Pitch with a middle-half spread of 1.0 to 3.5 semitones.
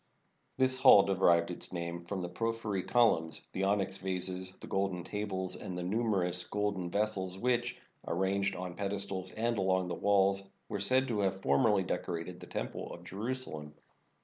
Yes: narrow, 2.5 semitones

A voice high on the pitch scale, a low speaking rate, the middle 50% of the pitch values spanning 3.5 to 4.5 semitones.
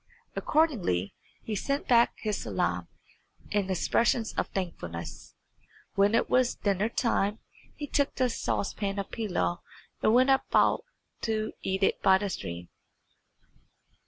Yes: high, 205 Hz; slow, 130 wpm; average, 3.9 semitones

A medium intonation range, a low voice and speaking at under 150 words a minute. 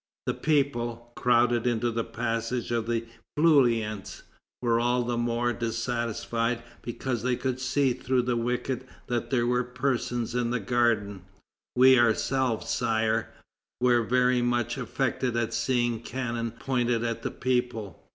No: narrow, 1.3 semitones; low, 120 Hz; average, 140 wpm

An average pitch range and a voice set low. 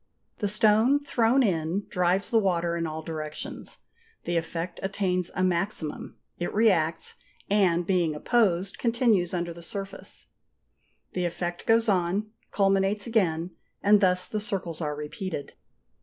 No: average, 3.5 semitones; medium, 185 Hz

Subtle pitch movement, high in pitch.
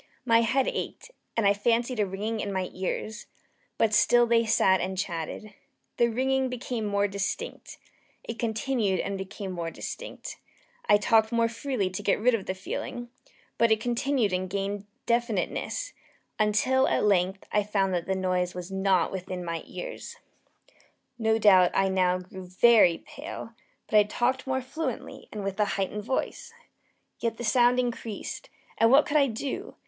No: average, 3.9 semitones; high, 215 Hz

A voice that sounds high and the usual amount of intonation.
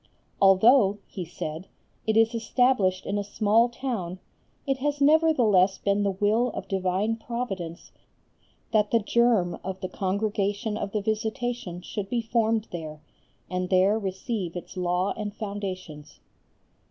Yes: high, 205 Hz; average, 3.5 semitones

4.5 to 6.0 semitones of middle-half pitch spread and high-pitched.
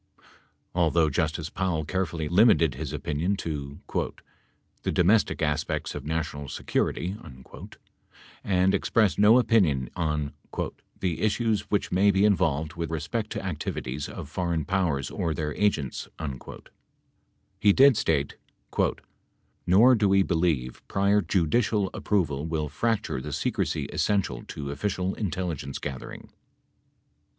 No: average, 4.8 semitones; very low, 85 Hz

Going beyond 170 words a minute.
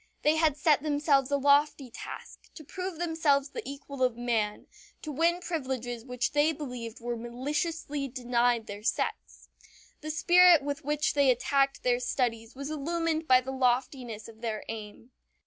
No: average, 160 wpm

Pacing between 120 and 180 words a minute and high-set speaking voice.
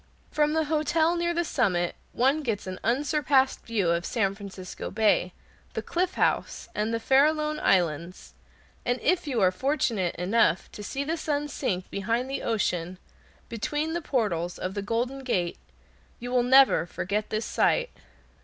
Yes: average, 160 wpm; high, 235 Hz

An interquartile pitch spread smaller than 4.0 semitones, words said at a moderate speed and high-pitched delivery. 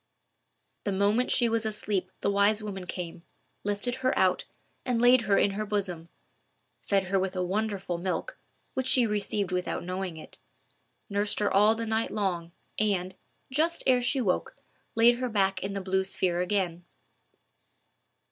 Yes: average, 3.1 semitones; average, 160 wpm; high, 200 Hz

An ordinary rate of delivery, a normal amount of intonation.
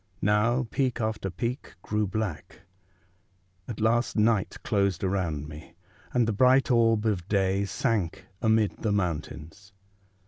No: slow, 130 wpm; average, 3.1 semitones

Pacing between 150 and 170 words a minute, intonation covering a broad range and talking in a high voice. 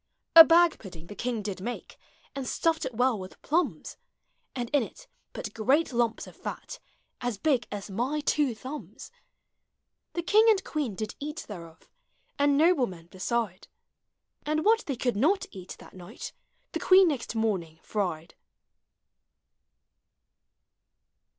No: average, 140 wpm; wide, 7.0 semitones; high, 245 Hz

